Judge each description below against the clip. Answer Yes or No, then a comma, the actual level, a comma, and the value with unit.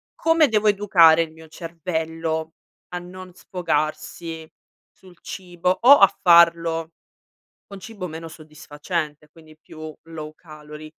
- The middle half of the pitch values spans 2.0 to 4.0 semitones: Yes, narrow, 2.5 semitones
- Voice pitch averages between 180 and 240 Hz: No, medium, 165 Hz